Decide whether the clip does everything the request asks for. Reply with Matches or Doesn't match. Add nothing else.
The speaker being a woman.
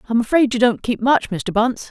Matches